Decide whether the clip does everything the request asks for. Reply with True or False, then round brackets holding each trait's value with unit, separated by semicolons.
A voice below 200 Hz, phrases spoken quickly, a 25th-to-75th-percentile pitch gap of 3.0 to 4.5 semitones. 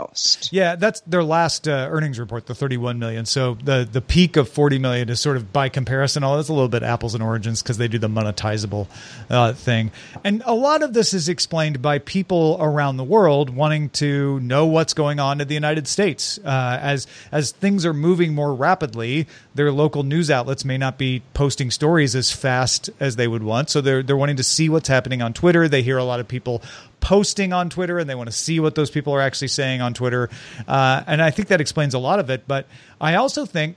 True (140 Hz; 225 wpm; 4.0 semitones)